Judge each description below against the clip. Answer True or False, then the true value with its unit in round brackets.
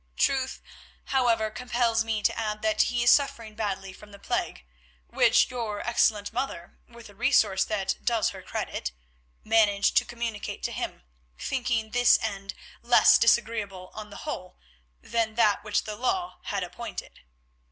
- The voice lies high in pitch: True (220 Hz)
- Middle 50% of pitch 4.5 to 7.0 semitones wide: False (2.6 semitones)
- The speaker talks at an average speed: True (150 wpm)